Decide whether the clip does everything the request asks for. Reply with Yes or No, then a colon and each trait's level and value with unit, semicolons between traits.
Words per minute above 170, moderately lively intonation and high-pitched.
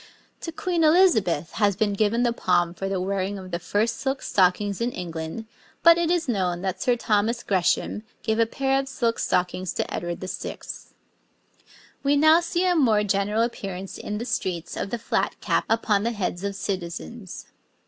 Yes: average, 180 wpm; average, 4.6 semitones; high, 210 Hz